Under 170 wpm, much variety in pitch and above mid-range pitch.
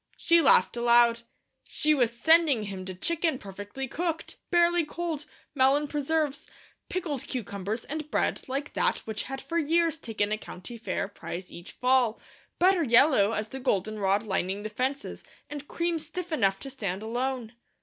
Yes: average, 160 wpm; wide, 6.4 semitones; very high, 260 Hz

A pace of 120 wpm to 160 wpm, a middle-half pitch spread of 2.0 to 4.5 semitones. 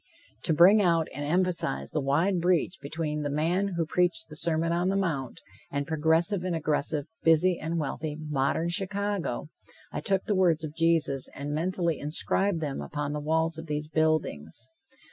No: average, 170 wpm; average, 2.9 semitones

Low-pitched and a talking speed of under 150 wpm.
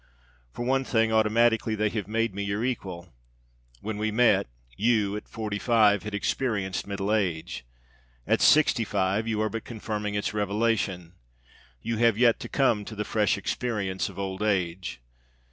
No: low, 105 Hz; average, 160 wpm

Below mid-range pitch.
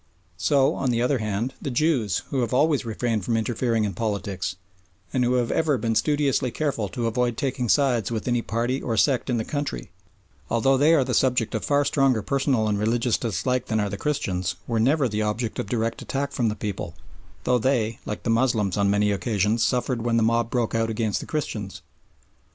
Yes: low, 115 Hz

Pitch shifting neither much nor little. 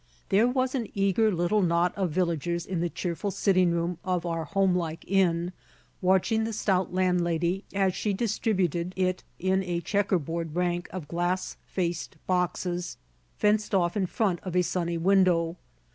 No: narrow, 2.1 semitones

